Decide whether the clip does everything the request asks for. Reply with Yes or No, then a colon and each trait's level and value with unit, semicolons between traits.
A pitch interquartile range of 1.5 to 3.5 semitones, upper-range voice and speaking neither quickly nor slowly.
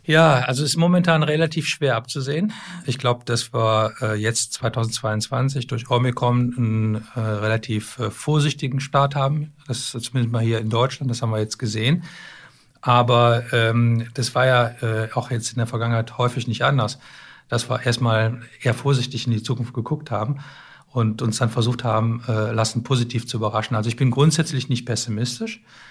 No: average, 2.8 semitones; low, 120 Hz; average, 175 wpm